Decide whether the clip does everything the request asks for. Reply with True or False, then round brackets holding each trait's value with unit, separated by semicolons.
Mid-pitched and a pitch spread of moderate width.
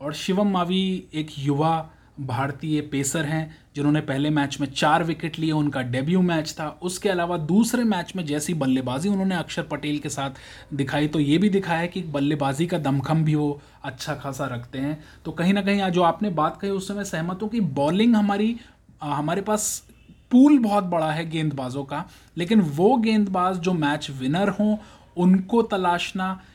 True (160 Hz; 4.6 semitones)